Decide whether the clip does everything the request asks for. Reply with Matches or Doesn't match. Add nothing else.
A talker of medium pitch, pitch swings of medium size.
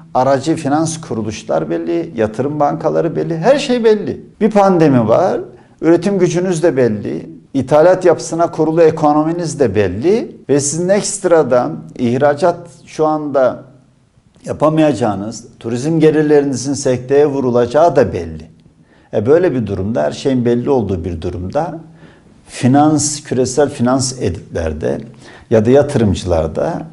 Matches